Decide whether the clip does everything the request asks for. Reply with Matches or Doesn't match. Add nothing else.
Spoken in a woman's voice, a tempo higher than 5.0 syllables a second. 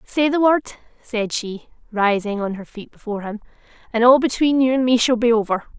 Matches